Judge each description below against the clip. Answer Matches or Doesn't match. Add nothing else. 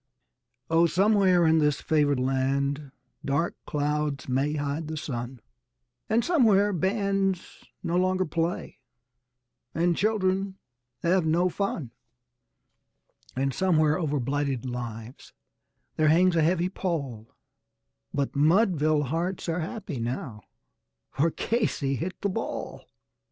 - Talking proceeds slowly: Matches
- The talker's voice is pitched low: Doesn't match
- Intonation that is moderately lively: Matches